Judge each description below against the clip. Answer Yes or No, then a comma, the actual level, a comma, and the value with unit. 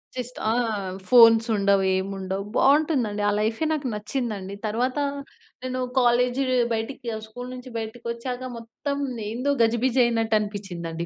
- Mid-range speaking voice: No, high, 230 Hz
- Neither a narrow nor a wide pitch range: Yes, average, 3.2 semitones